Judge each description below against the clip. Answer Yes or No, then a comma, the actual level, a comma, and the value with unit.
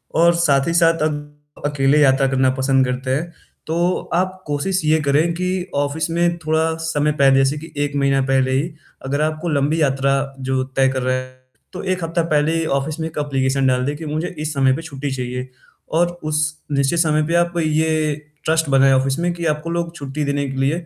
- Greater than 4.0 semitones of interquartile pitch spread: No, average, 3.4 semitones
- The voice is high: No, medium, 150 Hz